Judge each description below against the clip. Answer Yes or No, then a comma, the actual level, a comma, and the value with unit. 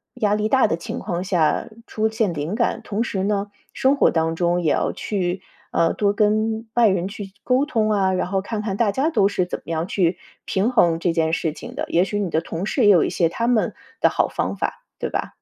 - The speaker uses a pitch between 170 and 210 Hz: Yes, high, 200 Hz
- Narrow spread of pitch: No, average, 3.9 semitones